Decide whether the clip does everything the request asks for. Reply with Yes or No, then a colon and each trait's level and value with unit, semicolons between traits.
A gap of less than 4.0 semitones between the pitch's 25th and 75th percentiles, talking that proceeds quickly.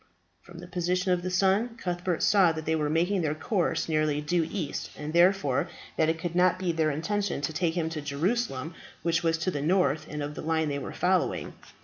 Yes: average, 2.9 semitones; fast, 215 wpm